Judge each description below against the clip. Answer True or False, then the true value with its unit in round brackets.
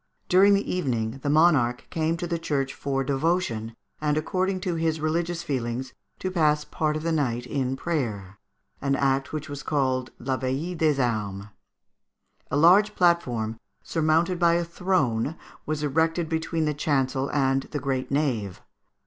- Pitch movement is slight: False (4.2 semitones)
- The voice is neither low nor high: True (150 Hz)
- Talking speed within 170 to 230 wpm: False (155 wpm)